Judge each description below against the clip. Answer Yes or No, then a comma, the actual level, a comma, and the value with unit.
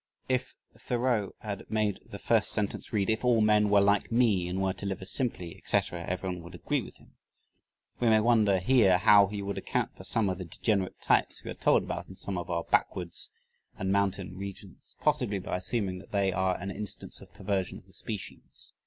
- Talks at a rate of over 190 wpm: Yes, fast, 205 wpm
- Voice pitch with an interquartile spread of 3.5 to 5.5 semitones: No, narrow, 2.5 semitones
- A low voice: Yes, low, 100 Hz